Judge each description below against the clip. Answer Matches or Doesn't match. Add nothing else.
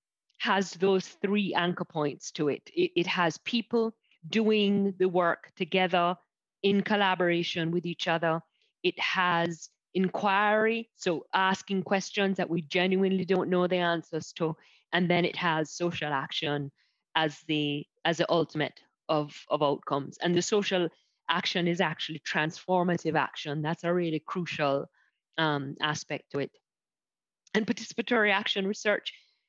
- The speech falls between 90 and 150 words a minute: Matches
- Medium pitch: Matches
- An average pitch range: Matches